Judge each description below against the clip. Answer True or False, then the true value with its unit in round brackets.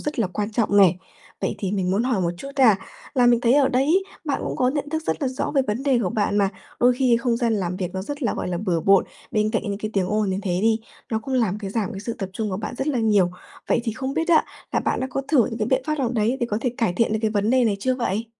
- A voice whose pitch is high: True (225 Hz)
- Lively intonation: False (4.2 semitones)